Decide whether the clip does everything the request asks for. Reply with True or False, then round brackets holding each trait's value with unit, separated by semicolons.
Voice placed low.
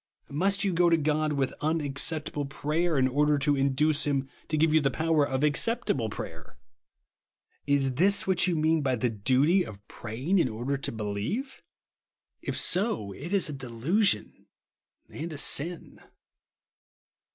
False (150 Hz)